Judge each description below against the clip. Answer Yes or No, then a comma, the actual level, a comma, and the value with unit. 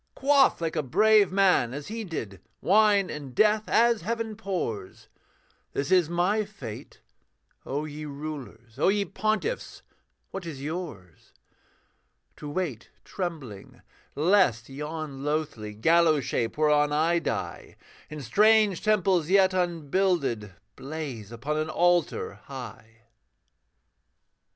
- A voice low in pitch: No, medium, 160 Hz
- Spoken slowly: Yes, slow, 115 wpm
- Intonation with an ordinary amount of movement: No, wide, 6.2 semitones